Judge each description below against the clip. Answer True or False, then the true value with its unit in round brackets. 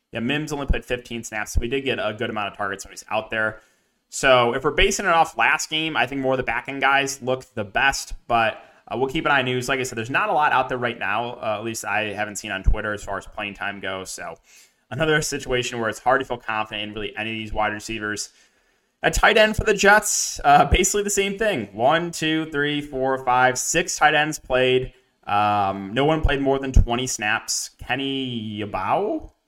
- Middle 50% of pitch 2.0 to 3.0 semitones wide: False (5.1 semitones)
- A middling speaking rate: False (240 wpm)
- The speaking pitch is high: False (125 Hz)